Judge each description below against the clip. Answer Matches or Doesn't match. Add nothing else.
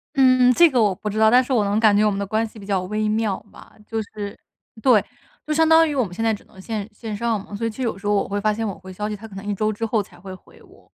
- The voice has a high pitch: Matches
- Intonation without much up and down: Matches